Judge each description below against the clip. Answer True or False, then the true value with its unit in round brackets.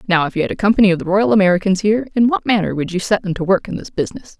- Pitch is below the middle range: False (195 Hz)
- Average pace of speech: False (315 wpm)